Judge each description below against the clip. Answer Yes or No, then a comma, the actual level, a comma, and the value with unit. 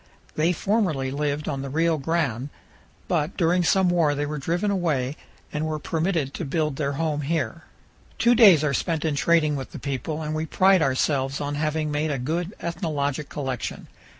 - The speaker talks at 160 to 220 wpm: Yes, average, 180 wpm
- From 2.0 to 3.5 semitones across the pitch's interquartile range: Yes, average, 2.9 semitones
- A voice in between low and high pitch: Yes, medium, 155 Hz